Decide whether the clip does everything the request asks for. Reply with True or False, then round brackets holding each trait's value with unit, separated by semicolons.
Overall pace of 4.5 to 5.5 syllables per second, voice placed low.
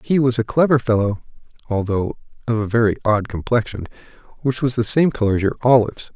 False (6.1 syllables/s; 120 Hz)